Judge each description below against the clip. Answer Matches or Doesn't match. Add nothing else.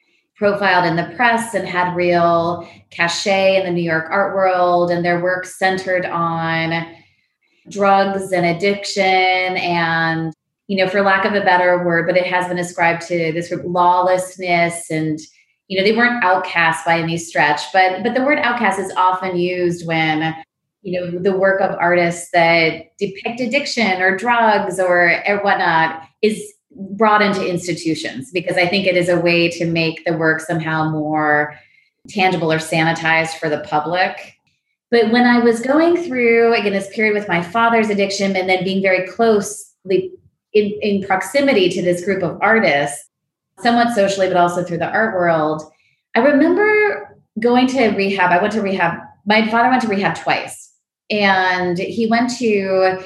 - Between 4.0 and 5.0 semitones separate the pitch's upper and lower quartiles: Doesn't match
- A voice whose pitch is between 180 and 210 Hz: Matches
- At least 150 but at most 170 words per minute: Matches